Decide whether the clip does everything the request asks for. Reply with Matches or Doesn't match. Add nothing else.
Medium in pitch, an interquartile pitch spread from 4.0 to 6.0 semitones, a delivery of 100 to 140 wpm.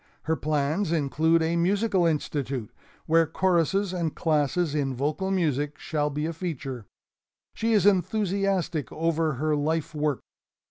Doesn't match